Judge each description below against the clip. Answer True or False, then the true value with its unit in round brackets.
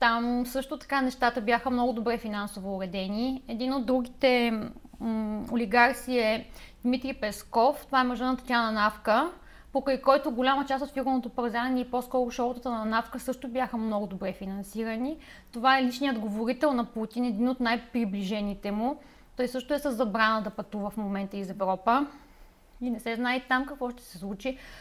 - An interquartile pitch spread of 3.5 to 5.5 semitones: False (2.8 semitones)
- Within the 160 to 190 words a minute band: True (165 wpm)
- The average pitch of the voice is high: True (245 Hz)